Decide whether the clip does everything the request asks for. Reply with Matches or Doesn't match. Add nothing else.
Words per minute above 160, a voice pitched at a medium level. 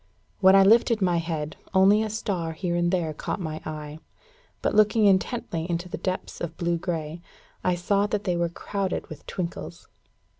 Matches